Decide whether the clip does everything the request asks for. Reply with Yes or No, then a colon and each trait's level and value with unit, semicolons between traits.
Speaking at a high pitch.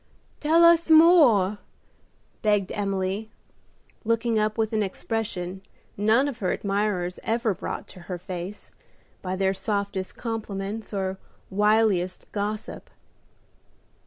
Yes: high, 205 Hz